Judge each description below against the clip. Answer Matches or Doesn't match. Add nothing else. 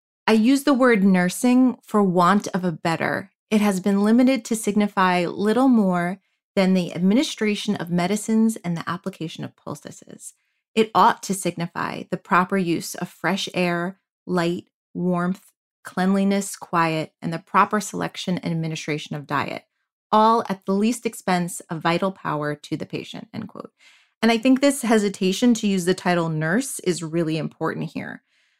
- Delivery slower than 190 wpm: Matches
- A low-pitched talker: Doesn't match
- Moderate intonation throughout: Matches